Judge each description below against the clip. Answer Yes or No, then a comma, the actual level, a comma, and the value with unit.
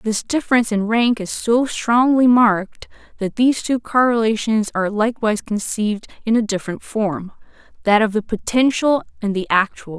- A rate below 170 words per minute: Yes, average, 150 wpm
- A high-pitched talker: Yes, high, 220 Hz